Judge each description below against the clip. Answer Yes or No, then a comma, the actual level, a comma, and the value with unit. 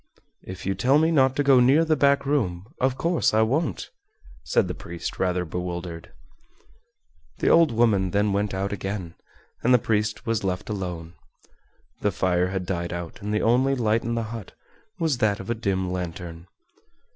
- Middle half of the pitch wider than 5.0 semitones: Yes, wide, 5.5 semitones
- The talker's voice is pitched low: Yes, low, 105 Hz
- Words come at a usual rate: Yes, average, 180 wpm